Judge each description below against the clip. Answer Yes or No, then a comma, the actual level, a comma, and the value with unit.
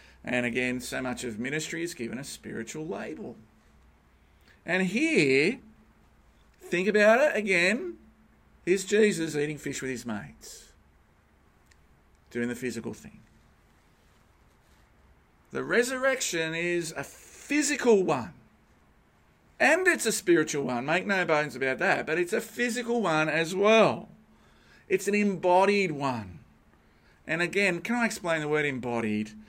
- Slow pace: Yes, slow, 130 wpm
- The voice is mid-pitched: Yes, medium, 165 Hz